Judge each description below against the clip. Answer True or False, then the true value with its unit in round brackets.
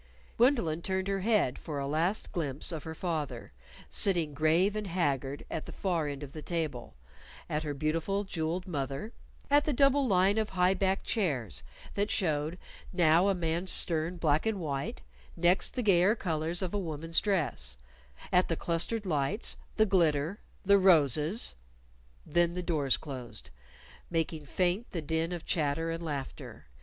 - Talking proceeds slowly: False (160 wpm)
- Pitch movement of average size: True (4.1 semitones)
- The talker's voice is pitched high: False (170 Hz)